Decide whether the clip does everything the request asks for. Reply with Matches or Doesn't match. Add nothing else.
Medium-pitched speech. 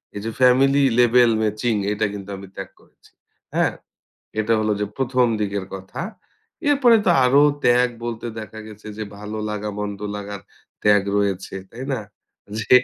Doesn't match